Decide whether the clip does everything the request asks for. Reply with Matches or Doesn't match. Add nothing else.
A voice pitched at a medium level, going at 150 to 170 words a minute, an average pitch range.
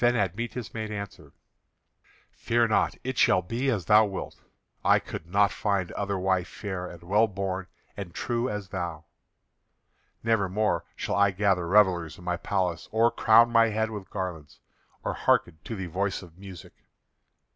Doesn't match